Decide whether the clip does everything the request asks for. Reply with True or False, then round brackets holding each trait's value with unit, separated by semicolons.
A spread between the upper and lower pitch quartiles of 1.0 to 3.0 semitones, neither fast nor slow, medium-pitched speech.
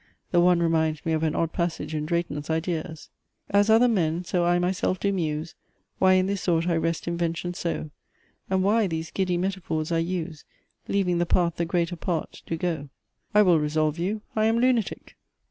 True (2.5 semitones; 190 wpm; 170 Hz)